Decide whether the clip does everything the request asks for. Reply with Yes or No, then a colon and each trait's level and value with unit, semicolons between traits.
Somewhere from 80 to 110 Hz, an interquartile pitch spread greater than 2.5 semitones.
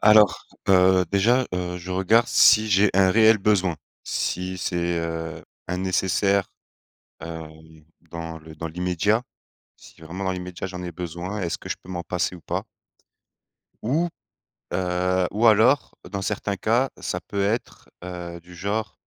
Yes: very low, 95 Hz; average, 2.9 semitones